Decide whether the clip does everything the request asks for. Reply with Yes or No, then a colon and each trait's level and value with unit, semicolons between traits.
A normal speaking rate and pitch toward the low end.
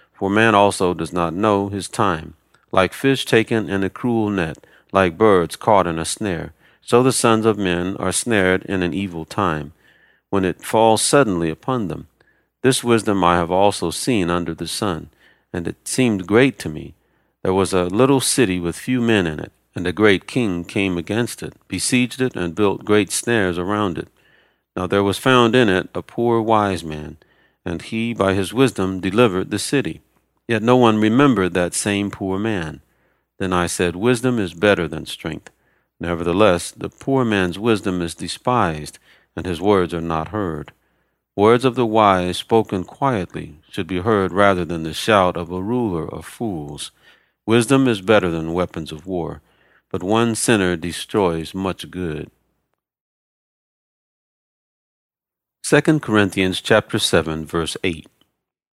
Yes: average, 165 wpm; low, 100 Hz